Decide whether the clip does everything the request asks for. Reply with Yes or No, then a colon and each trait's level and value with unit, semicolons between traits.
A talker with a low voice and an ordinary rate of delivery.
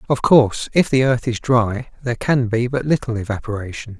Yes: low, 120 Hz; average, 195 wpm